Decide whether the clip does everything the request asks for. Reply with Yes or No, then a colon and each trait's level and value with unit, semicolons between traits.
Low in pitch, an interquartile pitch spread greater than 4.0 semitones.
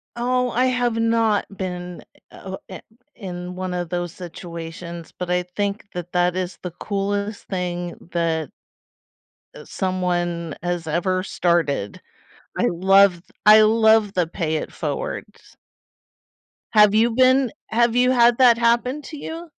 No: medium, 185 Hz; average, 4.5 semitones